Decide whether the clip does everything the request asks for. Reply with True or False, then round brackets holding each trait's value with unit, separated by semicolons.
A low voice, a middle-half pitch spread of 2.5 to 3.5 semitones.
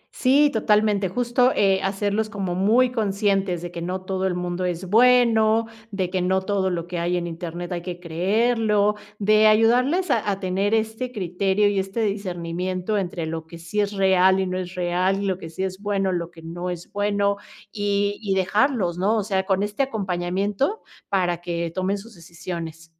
False (195 Hz; 2.9 semitones)